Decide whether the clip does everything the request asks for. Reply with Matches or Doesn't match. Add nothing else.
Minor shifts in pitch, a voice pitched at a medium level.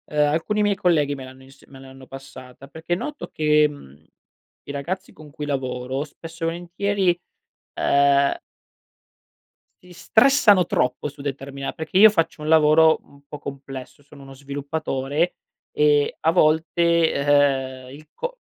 Doesn't match